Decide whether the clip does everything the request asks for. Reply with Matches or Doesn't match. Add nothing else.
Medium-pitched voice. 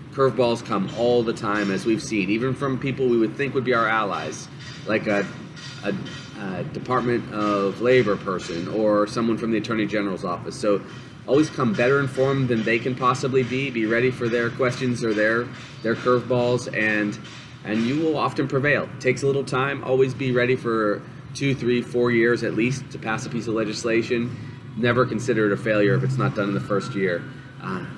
Doesn't match